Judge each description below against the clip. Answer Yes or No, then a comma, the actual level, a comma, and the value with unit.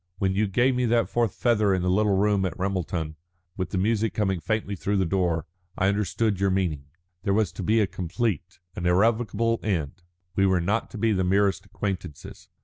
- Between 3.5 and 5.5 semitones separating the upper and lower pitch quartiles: No, average, 2.8 semitones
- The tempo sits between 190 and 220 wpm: Yes, average, 200 wpm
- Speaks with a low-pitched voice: Yes, very low, 95 Hz